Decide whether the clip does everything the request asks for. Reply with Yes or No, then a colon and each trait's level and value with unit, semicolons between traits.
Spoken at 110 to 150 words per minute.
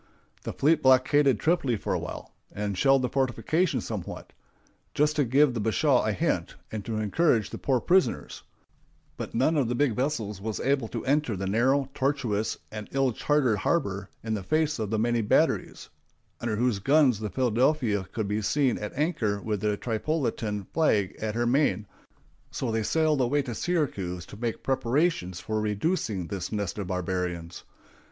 No: average, 175 wpm